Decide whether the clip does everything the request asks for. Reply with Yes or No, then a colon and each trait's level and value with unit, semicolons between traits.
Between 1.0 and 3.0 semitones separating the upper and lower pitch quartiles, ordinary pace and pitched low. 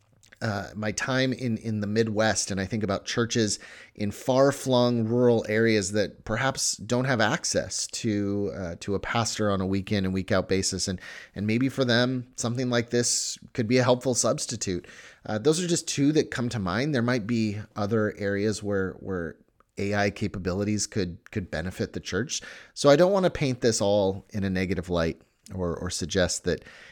No: average, 3.8 semitones; average, 190 wpm; low, 110 Hz